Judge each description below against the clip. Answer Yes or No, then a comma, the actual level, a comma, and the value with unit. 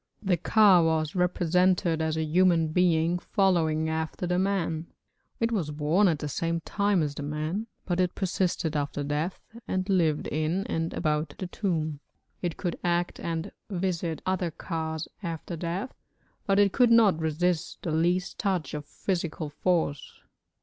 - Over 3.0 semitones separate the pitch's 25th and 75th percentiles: No, average, 2.7 semitones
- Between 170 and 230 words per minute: No, average, 155 wpm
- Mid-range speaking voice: Yes, medium, 170 Hz